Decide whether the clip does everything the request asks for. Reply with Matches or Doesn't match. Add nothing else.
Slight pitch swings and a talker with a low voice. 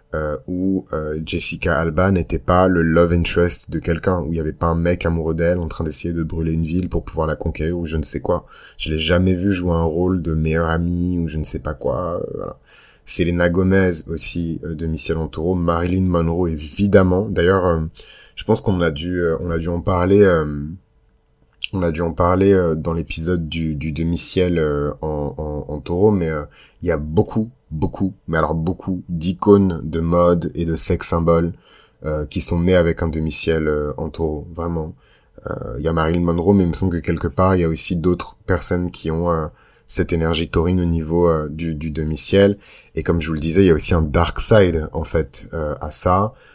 Matches